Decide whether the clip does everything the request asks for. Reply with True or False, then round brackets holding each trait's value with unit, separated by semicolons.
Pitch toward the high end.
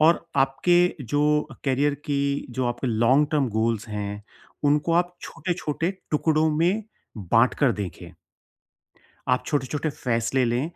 False (140 Hz)